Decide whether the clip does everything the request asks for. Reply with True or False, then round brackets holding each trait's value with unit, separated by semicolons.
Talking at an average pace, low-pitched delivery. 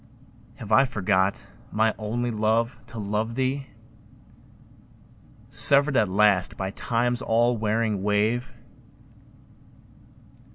False (95 wpm; 110 Hz)